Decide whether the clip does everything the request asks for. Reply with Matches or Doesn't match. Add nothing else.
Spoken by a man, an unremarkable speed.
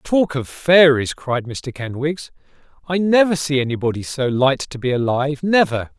Matches